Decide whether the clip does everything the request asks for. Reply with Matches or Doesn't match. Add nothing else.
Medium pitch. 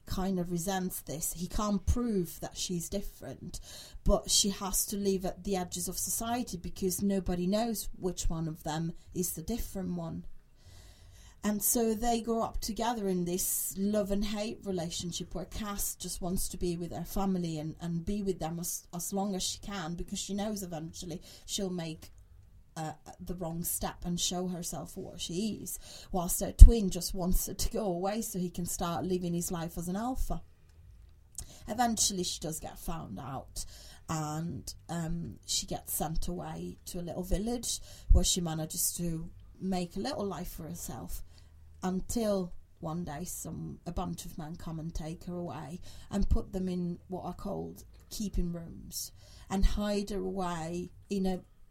Matches